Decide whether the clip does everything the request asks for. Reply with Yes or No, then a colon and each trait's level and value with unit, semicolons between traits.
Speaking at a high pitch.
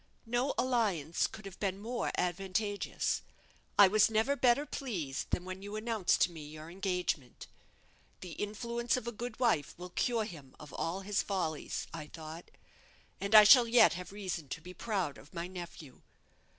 Yes: high, 195 Hz